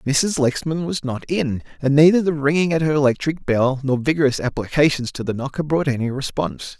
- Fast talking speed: No, average, 195 wpm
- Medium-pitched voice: Yes, medium, 145 Hz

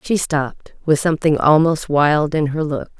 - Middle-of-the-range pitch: Yes, medium, 155 Hz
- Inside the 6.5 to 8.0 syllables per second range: No, 4.7 syllables/s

